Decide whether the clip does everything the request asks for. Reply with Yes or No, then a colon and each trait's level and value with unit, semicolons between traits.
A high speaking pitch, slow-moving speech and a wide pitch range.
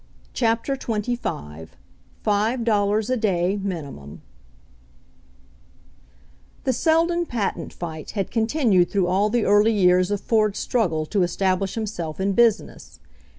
No: high, 205 Hz; slow, 115 wpm; average, 4.1 semitones